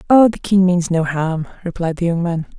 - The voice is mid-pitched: Yes, medium, 175 Hz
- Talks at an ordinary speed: No, fast, 230 wpm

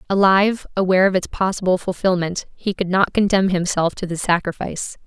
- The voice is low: No, medium, 185 Hz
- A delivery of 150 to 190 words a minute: Yes, average, 165 wpm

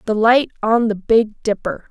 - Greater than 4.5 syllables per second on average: No, 4.4 syllables/s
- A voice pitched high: Yes, high, 220 Hz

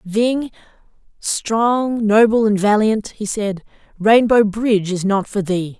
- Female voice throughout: Yes, female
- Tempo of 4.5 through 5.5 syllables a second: No, 3.7 syllables/s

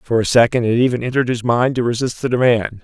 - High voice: No, low, 120 Hz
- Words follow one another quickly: Yes, fast, 255 wpm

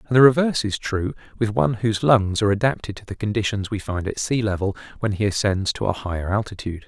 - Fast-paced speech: Yes, fast, 220 wpm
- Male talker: Yes, male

